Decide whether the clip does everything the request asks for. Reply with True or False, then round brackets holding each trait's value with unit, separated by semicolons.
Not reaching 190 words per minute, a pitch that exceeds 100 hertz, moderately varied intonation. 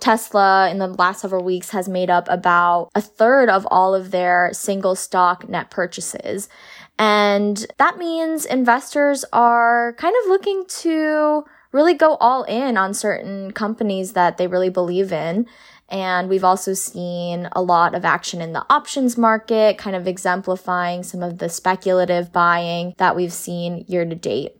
True (165 wpm; 190 Hz; 4.6 semitones)